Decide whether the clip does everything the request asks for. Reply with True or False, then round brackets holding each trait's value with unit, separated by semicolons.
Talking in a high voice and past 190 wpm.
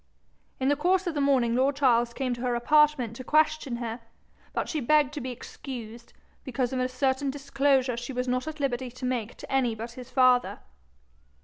True (255 Hz; 200 wpm)